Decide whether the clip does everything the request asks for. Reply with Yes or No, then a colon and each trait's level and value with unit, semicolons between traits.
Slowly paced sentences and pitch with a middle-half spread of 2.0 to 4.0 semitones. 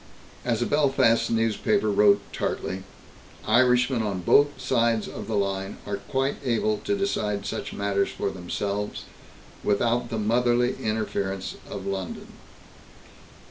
Yes: slow, 125 wpm; average, 3.3 semitones